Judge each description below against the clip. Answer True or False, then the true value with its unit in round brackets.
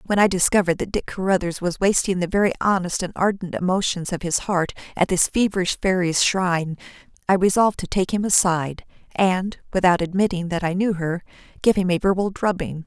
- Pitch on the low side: False (185 Hz)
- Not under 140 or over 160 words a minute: False (185 wpm)